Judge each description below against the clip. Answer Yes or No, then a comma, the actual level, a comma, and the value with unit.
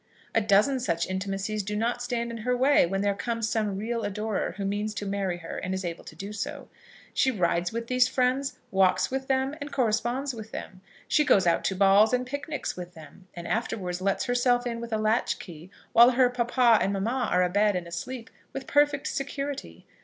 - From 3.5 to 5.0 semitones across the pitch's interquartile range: Yes, average, 4.4 semitones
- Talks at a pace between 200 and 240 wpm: Yes, fast, 205 wpm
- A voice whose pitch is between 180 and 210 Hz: No, high, 220 Hz